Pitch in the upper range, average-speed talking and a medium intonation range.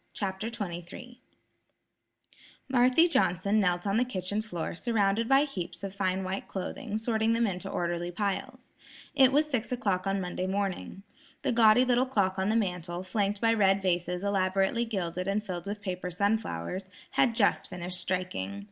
Yes: high, 195 Hz; average, 160 wpm; average, 3.7 semitones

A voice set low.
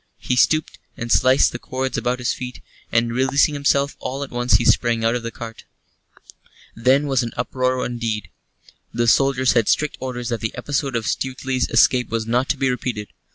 Yes: low, 125 Hz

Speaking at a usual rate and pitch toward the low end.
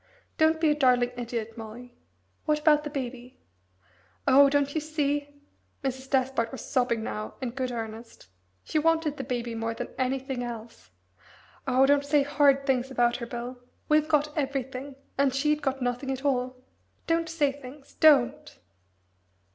No: average, 155 wpm; very high, 265 Hz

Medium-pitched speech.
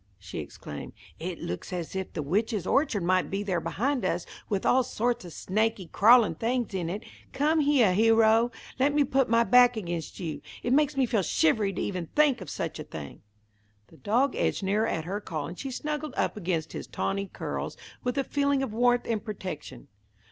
No: high, 215 Hz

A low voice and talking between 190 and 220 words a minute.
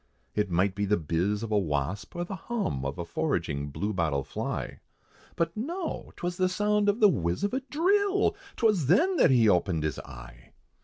Yes: low, 105 Hz; average, 195 wpm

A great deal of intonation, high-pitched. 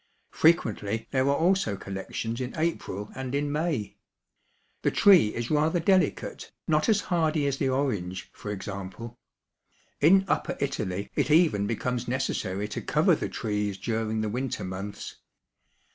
No: wide, 6.8 semitones; low, 125 Hz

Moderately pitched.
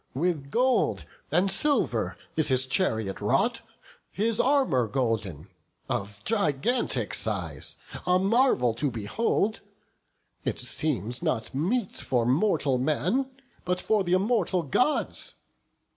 Yes: medium, 165 Hz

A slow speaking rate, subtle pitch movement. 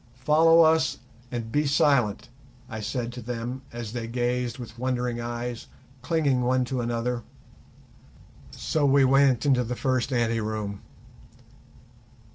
Yes: slow, 130 wpm; narrow, 2.2 semitones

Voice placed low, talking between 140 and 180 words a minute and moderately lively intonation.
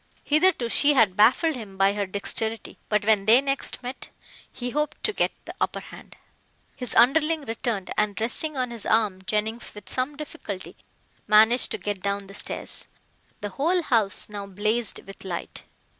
No: high, 225 Hz; average, 170 wpm; average, 4.7 semitones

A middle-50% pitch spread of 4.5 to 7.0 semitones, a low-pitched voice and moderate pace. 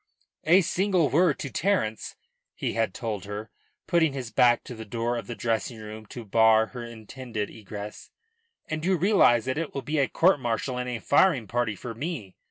Yes: average, 5.2 semitones; low, 120 Hz; average, 190 wpm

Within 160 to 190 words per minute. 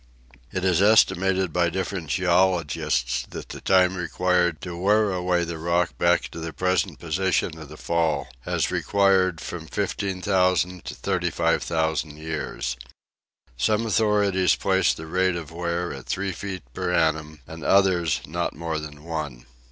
No: average, 145 wpm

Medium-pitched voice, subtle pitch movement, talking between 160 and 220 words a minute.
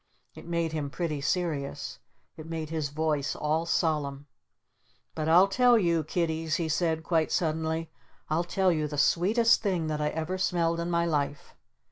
Yes: medium, 160 Hz; narrow, 1.9 semitones; average, 165 wpm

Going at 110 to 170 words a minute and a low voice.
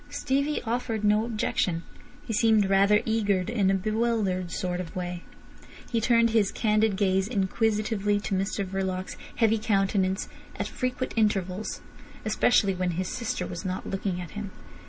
No: average, 150 wpm; high, 205 Hz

